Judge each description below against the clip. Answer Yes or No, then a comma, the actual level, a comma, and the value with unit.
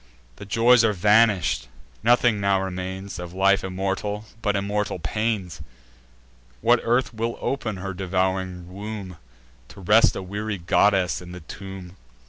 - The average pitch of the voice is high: No, low, 100 Hz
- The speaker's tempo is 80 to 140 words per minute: Yes, slow, 135 wpm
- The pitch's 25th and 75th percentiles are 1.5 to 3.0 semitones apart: Yes, narrow, 2.5 semitones